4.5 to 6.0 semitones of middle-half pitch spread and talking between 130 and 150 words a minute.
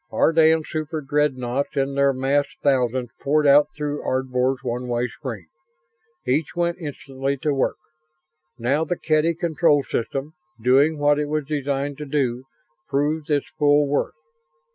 No: narrow, 2.4 semitones; average, 140 wpm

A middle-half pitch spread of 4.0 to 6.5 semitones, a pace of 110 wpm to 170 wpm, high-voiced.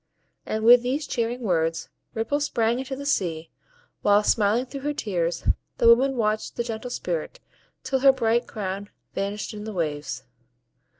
Yes: average, 4.3 semitones; average, 160 wpm; high, 225 Hz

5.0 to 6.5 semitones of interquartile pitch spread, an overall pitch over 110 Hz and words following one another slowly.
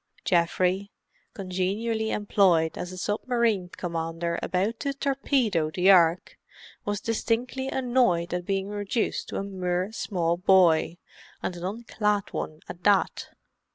No: average, 3.9 semitones; high, 190 Hz; slow, 125 wpm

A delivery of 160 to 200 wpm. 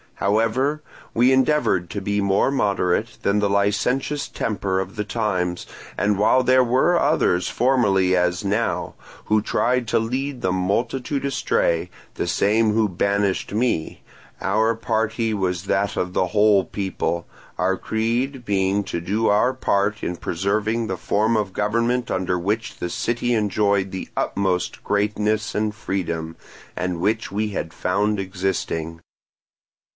No: average, 140 wpm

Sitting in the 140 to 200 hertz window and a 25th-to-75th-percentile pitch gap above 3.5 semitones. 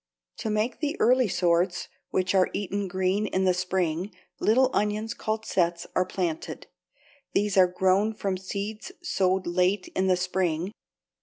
No: high, 190 Hz; narrow, 2.5 semitones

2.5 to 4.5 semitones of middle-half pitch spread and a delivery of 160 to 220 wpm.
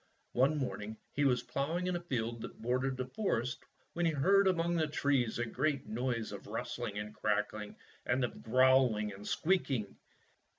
No: average, 4.9 semitones; average, 175 wpm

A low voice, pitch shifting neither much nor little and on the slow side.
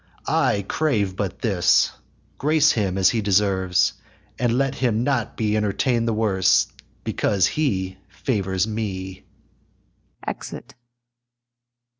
Yes: low, 105 Hz; average, 3.9 semitones; slow, 110 wpm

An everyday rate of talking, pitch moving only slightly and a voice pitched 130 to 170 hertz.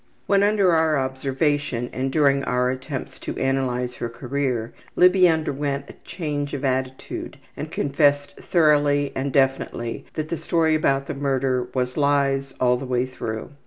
Yes: average, 155 wpm; narrow, 2.3 semitones; medium, 140 Hz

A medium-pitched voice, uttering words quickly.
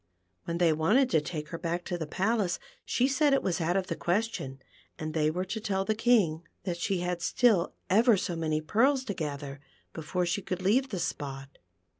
Yes: medium, 180 Hz; fast, 210 wpm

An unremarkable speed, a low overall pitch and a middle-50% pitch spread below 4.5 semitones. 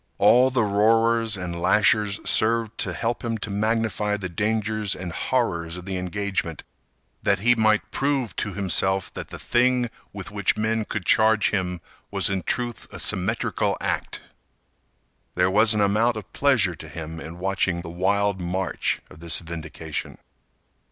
Yes: average, 165 wpm; low, 105 Hz; average, 3.8 semitones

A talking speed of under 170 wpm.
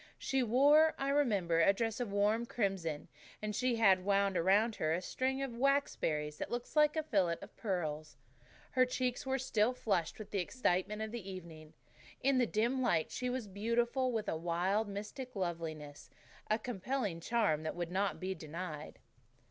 No: average, 180 wpm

